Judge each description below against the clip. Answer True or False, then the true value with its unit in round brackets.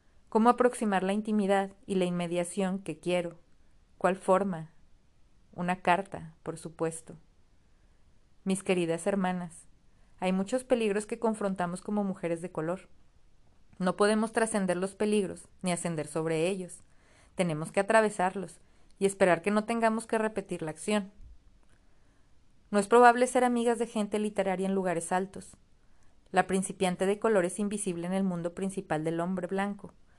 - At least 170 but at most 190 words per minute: False (145 wpm)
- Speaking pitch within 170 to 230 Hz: True (190 Hz)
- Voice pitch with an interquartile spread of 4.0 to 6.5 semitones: False (2.9 semitones)